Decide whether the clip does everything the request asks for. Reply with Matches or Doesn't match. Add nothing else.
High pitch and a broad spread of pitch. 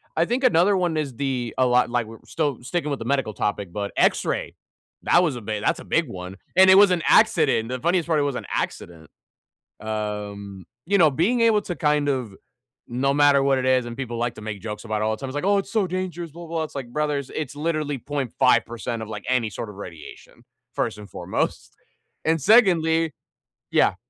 Doesn't match